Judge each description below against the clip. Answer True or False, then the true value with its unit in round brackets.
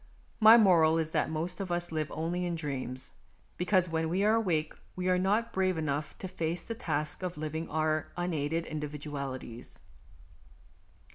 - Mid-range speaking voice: True (165 Hz)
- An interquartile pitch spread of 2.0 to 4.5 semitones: True (3.0 semitones)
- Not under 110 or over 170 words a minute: True (165 wpm)